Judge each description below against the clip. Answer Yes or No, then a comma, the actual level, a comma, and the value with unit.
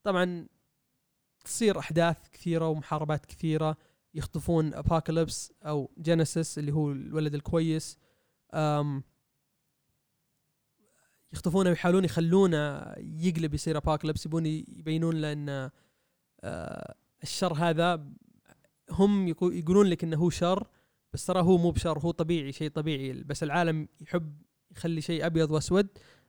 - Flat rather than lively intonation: Yes, narrow, 2.1 semitones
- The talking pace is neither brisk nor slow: Yes, average, 110 wpm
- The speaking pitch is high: No, medium, 165 Hz